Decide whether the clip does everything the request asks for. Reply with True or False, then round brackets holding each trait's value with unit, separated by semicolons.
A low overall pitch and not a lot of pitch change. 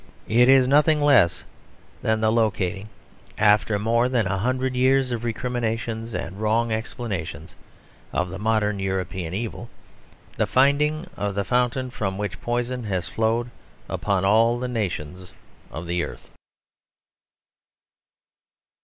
False (110 Hz; 4.1 semitones)